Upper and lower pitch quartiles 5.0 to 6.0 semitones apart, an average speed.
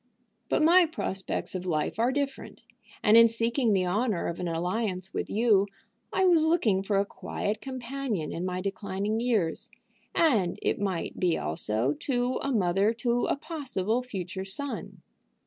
Yes: average, 5.3 semitones; average, 160 wpm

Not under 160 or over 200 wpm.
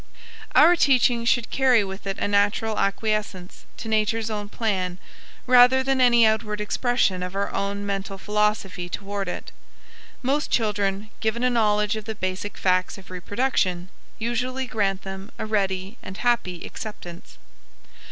No: average, 145 wpm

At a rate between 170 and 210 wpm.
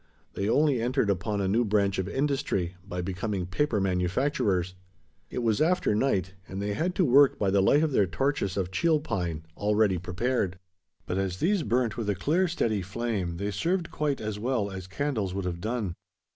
Yes: average, 190 wpm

